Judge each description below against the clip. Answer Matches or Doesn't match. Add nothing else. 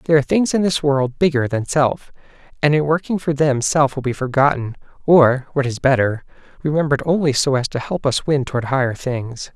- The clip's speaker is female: Doesn't match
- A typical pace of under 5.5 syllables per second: Doesn't match